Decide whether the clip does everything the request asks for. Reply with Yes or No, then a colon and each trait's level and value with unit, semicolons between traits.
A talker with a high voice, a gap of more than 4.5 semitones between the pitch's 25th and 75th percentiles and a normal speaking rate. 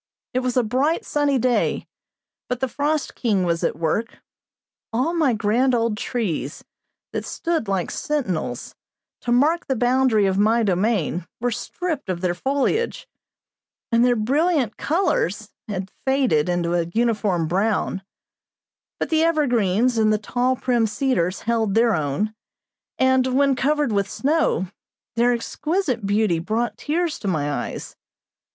Yes: high, 235 Hz; average, 5.2 semitones; average, 145 wpm